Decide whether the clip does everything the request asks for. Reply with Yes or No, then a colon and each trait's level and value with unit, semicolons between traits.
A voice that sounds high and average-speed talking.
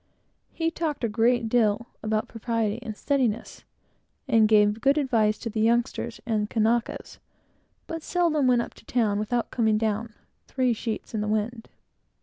Yes: high, 230 Hz; average, 160 wpm